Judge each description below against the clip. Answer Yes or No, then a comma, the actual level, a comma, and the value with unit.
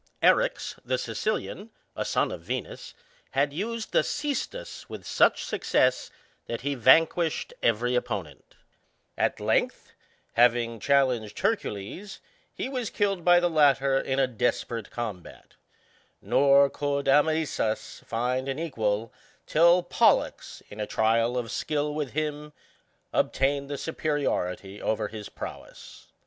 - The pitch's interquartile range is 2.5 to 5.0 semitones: No, wide, 5.5 semitones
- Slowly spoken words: Yes, slow, 125 wpm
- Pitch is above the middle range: No, medium, 140 Hz